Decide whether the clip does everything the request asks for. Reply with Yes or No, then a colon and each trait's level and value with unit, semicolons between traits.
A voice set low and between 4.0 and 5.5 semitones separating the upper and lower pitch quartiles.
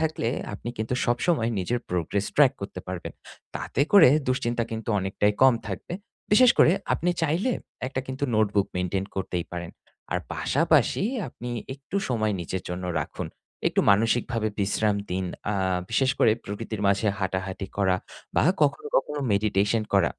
Yes: low, 110 Hz; average, 5.2 semitones